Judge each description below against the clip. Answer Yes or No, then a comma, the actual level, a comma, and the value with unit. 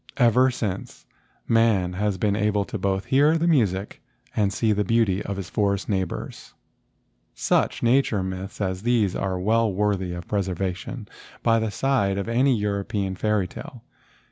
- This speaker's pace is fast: No, average, 165 wpm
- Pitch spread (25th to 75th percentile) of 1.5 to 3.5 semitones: Yes, average, 3.1 semitones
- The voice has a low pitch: Yes, low, 105 Hz